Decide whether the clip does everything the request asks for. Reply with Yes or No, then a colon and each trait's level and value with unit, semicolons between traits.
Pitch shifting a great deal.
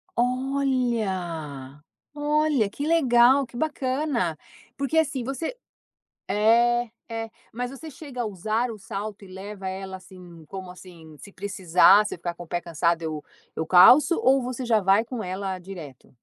Yes: wide, 5.9 semitones